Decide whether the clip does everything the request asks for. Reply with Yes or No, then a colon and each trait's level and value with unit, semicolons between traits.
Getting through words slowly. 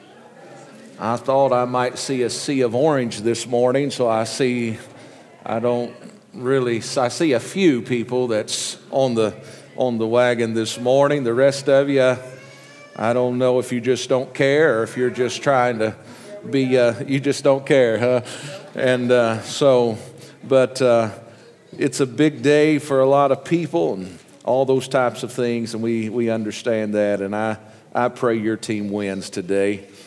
No: average, 175 wpm